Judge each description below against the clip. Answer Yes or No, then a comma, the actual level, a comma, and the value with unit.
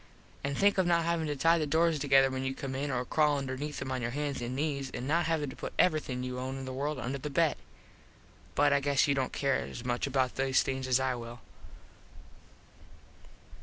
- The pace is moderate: No, fast, 225 wpm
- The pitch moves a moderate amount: No, narrow, 2.3 semitones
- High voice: No, low, 135 Hz